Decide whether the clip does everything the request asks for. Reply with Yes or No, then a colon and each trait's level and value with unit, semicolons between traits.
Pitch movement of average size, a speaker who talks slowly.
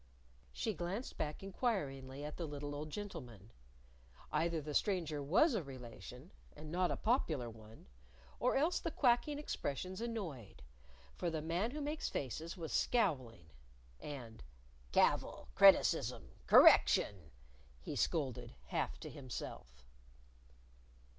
No: wide, 7.2 semitones; slow, 120 wpm